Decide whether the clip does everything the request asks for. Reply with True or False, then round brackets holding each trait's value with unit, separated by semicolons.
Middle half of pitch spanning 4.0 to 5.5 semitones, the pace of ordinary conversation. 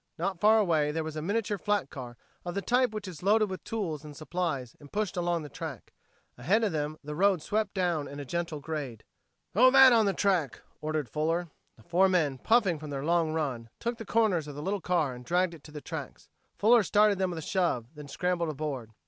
False (5.0 semitones; 225 wpm)